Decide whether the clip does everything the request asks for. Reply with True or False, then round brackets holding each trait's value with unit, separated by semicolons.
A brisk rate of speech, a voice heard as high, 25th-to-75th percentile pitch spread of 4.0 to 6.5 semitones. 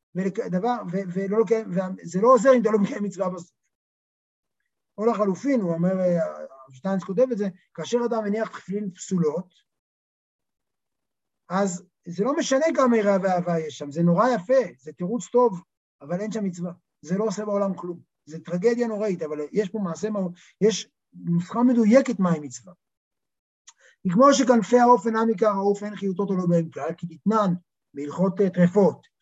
True (160 wpm; 195 Hz; 4.5 semitones)